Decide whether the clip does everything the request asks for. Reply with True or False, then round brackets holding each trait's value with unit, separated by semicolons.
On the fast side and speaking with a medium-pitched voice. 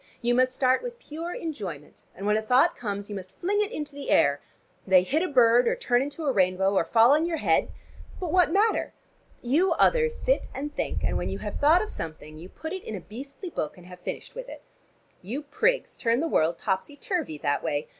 False (225 wpm; 255 Hz)